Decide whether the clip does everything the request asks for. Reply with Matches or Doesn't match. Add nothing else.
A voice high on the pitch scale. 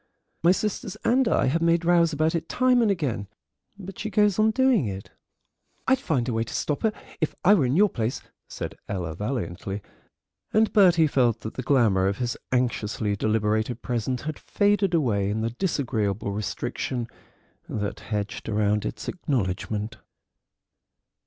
Doesn't match